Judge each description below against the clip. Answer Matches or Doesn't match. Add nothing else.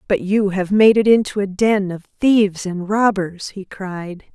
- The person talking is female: Matches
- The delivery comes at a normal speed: Matches